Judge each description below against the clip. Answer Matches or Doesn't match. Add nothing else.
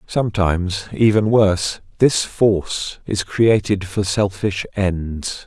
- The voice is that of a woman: Doesn't match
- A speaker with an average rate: Doesn't match